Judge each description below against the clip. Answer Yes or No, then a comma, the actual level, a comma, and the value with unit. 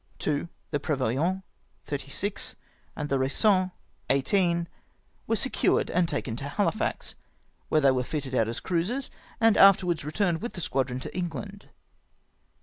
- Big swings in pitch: Yes, wide, 5.9 semitones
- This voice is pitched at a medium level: Yes, medium, 165 Hz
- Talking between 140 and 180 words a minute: Yes, average, 145 wpm